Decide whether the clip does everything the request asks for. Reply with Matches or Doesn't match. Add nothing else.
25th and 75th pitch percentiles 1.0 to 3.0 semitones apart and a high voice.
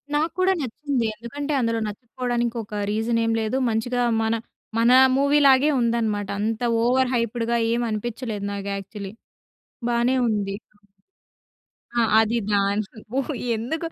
Matches